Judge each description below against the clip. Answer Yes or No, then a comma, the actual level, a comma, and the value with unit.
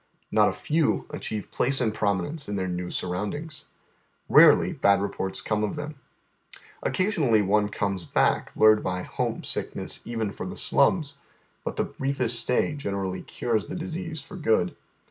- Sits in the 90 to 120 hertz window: Yes, low, 110 Hz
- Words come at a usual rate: Yes, average, 155 wpm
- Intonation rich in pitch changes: Yes, wide, 6.9 semitones